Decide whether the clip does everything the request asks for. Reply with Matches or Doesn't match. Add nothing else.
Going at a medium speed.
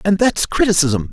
Matches